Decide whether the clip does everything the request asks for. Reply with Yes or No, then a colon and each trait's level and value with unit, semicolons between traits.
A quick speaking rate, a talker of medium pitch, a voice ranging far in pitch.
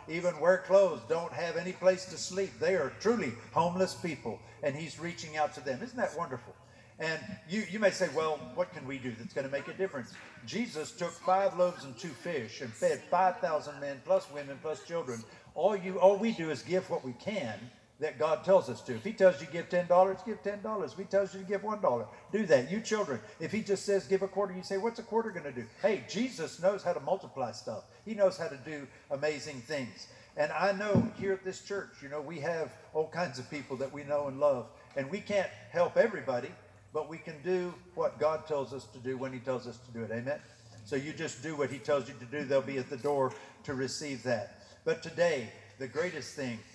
Yes: fast, 235 wpm; medium, 160 Hz; wide, 5.7 semitones